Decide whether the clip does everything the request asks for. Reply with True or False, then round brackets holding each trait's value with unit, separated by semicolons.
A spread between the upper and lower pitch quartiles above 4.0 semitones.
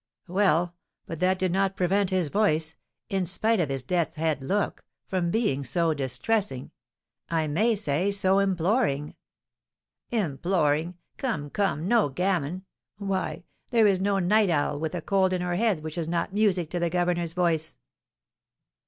False (3.7 semitones)